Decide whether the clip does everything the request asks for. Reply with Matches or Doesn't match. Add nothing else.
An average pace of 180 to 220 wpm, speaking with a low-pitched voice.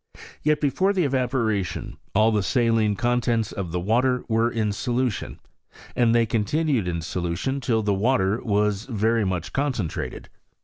Doesn't match